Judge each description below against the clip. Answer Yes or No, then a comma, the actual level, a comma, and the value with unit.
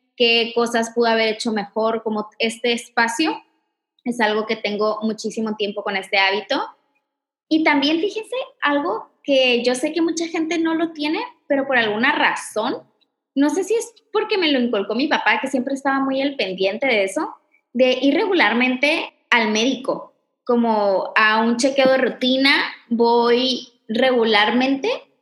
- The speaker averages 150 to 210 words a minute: Yes, average, 155 wpm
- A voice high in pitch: Yes, very high, 255 Hz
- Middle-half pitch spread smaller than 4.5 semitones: No, average, 4.9 semitones